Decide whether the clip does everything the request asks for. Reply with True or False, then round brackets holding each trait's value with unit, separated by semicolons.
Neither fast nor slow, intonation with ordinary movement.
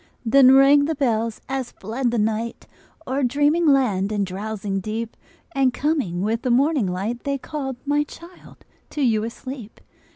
True (160 wpm; 4.4 semitones)